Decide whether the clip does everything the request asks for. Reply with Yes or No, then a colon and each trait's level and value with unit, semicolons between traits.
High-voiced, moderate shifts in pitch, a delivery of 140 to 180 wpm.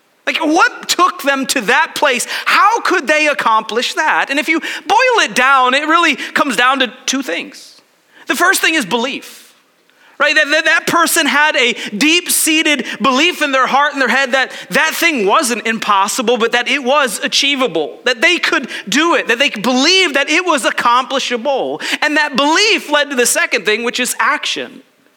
No: very high, 285 Hz; average, 3.9 semitones; average, 190 wpm